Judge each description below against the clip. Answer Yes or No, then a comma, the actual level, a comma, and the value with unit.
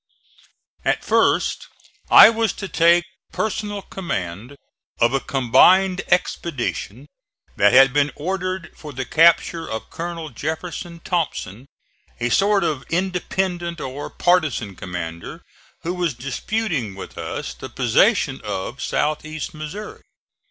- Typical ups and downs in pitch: No, wide, 5.8 semitones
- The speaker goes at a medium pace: No, slow, 120 wpm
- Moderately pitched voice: Yes, medium, 160 Hz